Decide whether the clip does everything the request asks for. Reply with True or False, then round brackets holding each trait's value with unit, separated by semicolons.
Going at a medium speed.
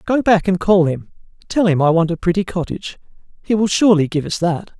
False (225 wpm)